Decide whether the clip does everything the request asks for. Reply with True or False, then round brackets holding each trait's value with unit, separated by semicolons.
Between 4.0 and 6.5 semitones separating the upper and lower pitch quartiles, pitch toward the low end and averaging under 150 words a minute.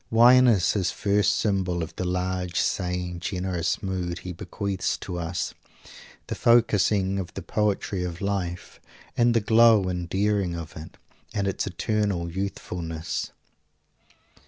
False (2.6 semitones; 95 Hz; 135 wpm)